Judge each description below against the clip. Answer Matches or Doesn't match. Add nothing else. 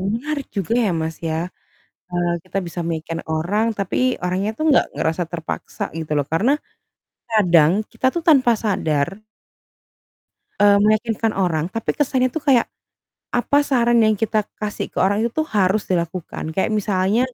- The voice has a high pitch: Matches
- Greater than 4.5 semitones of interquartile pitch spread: Matches